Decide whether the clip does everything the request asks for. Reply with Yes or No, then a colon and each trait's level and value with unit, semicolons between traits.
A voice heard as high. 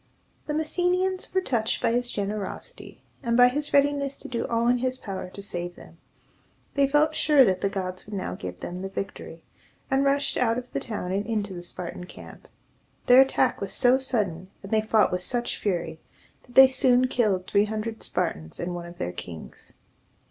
Yes: high, 225 Hz